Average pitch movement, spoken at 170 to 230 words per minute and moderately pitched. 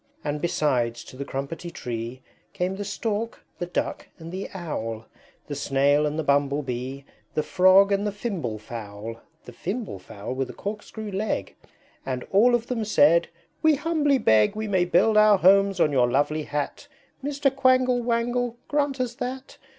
No: wide, 8.7 semitones; average, 175 wpm; medium, 180 Hz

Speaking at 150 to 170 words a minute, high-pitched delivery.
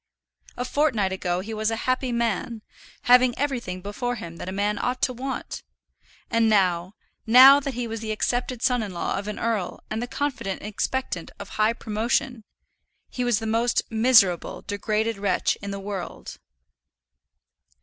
Yes: average, 165 wpm; high, 225 Hz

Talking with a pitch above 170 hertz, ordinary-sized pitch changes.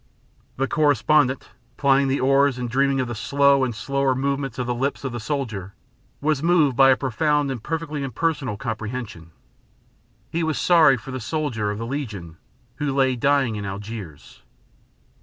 No: low, 135 Hz; average, 3.6 semitones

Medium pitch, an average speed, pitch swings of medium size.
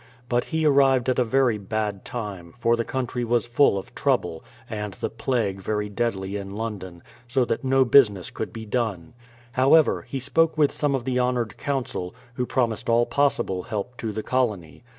No: low, 120 Hz; average, 190 wpm; average, 3.9 semitones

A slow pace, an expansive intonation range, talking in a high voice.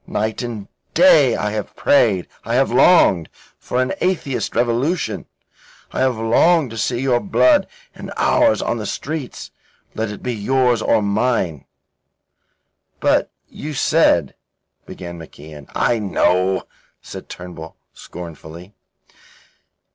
No: slow, 125 wpm; wide, 6.0 semitones; low, 115 Hz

